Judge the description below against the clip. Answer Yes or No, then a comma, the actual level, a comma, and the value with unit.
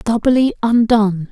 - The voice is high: Yes, high, 225 Hz